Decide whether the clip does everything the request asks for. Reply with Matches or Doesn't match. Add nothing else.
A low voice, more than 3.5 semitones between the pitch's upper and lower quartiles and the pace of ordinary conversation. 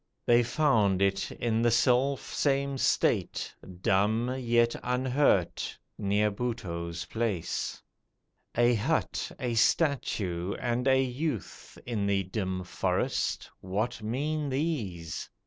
Doesn't match